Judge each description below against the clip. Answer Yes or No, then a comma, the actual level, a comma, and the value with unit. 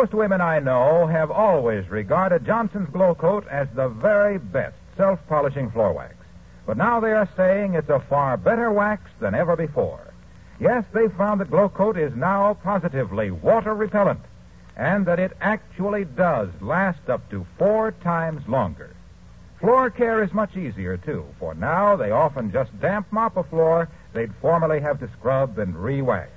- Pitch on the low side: No, medium, 180 Hz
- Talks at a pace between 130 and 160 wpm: No, average, 170 wpm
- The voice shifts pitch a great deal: Yes, wide, 6.5 semitones